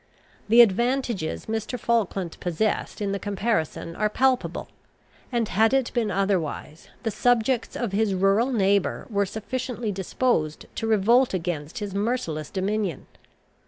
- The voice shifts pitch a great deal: No, average, 3.7 semitones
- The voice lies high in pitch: Yes, high, 210 Hz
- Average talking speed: No, slow, 130 wpm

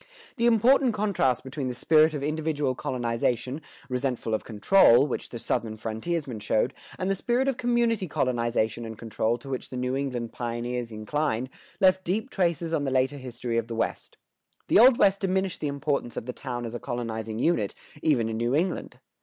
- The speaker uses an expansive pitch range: Yes, wide, 6.4 semitones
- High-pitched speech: No, low, 130 Hz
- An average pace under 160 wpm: No, average, 185 wpm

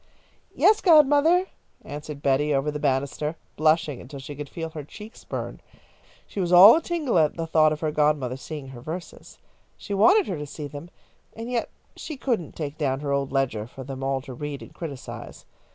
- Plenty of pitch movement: No, average, 4.9 semitones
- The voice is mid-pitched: Yes, medium, 150 Hz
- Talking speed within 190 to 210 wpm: Yes, average, 195 wpm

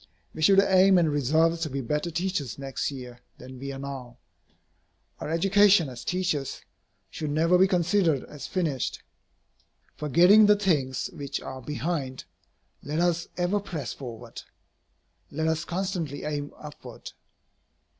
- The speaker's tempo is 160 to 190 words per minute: No, slow, 135 wpm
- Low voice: No, medium, 155 Hz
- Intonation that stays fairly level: No, average, 4.6 semitones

